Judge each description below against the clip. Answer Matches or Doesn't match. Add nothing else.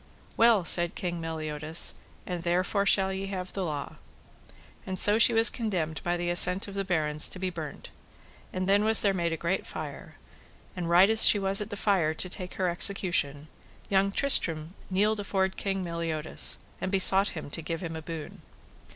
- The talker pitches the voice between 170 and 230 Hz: Matches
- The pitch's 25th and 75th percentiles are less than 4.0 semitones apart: Matches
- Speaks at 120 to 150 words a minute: Doesn't match